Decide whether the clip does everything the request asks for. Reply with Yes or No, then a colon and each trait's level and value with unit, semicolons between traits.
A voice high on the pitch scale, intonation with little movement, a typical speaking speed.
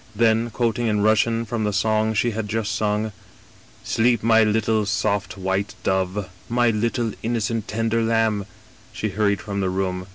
No: low, 110 Hz; narrow, 1.9 semitones; average, 165 wpm